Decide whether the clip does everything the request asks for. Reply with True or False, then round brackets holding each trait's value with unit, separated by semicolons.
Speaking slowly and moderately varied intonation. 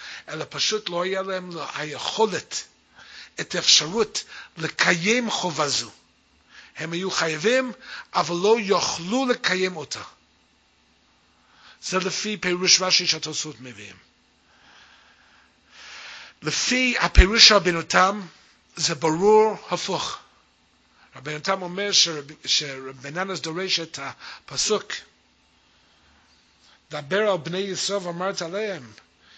False (90 wpm; 7.9 semitones)